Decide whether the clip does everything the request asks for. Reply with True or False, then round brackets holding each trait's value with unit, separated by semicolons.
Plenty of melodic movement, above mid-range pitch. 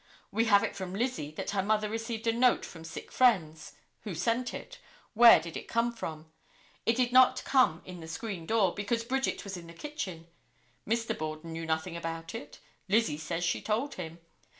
True (6.0 semitones; 200 Hz)